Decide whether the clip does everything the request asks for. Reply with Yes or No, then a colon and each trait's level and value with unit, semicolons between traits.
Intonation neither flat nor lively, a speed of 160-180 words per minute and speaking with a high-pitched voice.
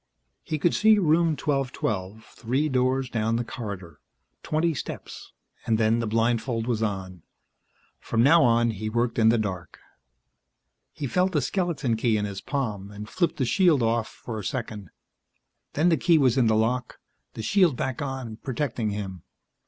No: average, 4.4 semitones; average, 170 wpm; low, 120 Hz